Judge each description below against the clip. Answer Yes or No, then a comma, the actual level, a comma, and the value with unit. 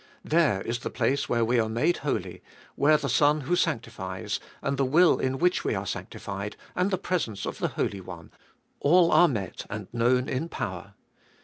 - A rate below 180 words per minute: No, average, 190 wpm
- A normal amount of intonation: No, wide, 6.4 semitones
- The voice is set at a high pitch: No, low, 130 Hz